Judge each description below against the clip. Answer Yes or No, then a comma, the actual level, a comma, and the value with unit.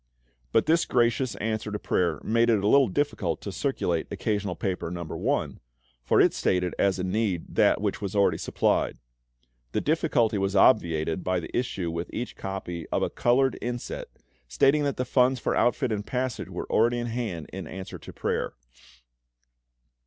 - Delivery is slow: No, average, 175 wpm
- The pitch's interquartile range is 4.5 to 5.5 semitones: Yes, average, 5.1 semitones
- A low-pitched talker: Yes, low, 105 Hz